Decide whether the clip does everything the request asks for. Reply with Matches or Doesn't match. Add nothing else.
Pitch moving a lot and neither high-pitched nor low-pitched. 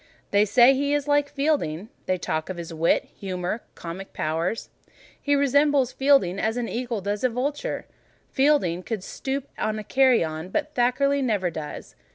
Doesn't match